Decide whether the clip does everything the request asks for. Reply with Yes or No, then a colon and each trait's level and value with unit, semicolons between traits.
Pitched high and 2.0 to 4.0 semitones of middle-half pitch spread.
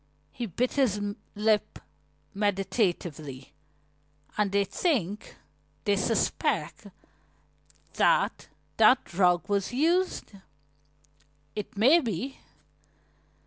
No: high, 210 Hz; average, 4.4 semitones